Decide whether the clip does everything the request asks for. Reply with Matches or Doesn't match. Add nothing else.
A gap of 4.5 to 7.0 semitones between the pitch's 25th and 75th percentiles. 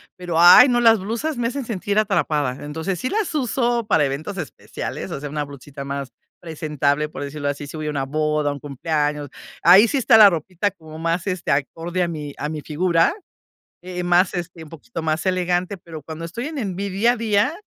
Matches